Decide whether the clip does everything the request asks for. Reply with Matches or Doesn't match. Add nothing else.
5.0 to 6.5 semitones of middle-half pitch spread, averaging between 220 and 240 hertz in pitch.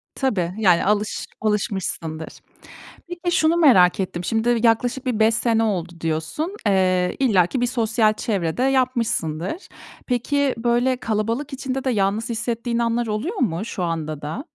Matches